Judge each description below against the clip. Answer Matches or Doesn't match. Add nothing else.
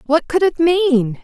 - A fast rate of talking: Doesn't match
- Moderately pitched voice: Doesn't match